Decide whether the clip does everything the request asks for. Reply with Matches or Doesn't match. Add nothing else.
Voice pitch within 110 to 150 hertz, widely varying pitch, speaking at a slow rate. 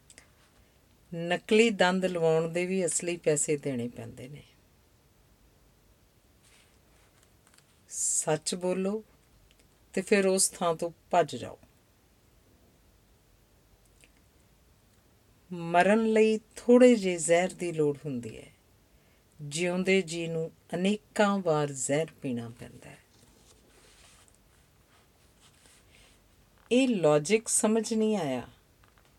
Doesn't match